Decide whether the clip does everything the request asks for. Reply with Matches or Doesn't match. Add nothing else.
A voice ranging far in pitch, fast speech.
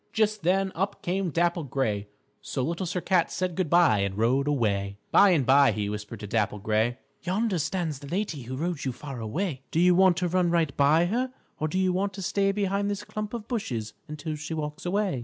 Matches